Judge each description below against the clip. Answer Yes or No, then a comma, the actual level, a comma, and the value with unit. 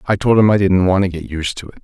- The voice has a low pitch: Yes, very low, 95 Hz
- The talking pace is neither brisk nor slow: No, fast, 360 wpm